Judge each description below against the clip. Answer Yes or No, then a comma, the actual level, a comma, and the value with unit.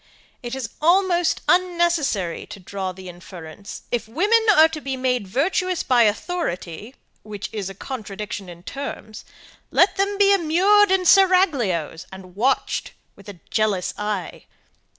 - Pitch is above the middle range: Yes, high, 245 Hz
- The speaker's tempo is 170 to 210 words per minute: No, average, 140 wpm